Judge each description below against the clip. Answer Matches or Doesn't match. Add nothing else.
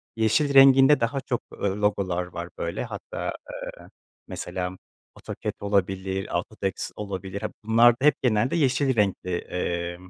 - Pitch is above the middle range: Doesn't match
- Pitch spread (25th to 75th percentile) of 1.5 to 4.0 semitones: Doesn't match